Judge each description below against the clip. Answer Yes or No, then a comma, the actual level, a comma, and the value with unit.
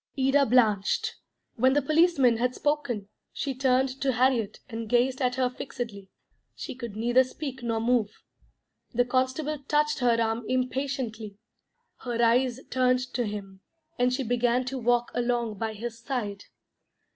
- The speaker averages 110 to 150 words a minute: Yes, average, 145 wpm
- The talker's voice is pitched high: Yes, high, 245 Hz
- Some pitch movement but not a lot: No, narrow, 2.3 semitones